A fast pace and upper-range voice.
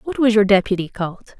Yes: fast, 215 wpm; high, 210 Hz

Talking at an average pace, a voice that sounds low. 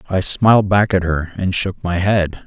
No: fast, 220 wpm; very low, 95 Hz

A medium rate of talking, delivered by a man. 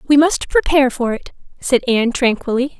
No: average, 170 wpm; female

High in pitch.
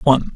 No: low, 135 Hz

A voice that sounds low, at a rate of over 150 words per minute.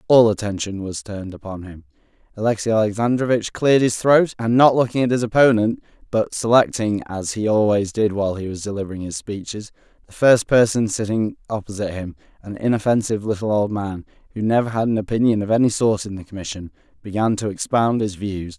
Yes: low, 105 Hz; average, 180 wpm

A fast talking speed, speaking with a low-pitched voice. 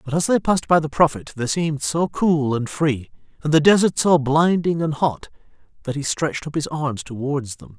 No: fast, 215 wpm; medium, 150 Hz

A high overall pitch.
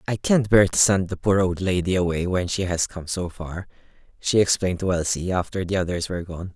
No: very low, 90 Hz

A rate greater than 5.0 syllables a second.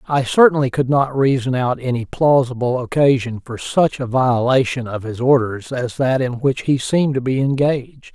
No: 4.9 syllables/s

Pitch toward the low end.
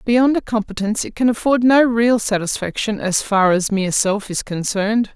No: high, 215 Hz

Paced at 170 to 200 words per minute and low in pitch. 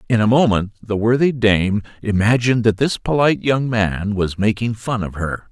Yes: average, 185 wpm; low, 110 Hz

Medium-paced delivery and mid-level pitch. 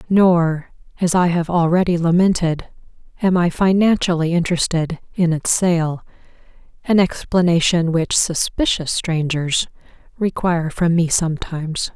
No: slow, 110 wpm; medium, 170 Hz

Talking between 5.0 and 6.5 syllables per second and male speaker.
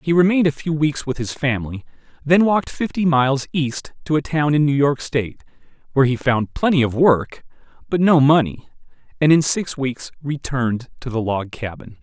Yes: 5.4 syllables/s; male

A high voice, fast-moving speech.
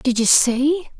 No: very high, 270 Hz; average, 180 wpm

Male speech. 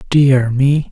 Yes: male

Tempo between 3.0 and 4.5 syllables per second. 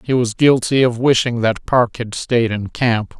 Yes: 4.2 syllables/s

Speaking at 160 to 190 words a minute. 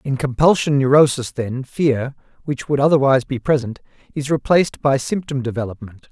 No: average, 145 wpm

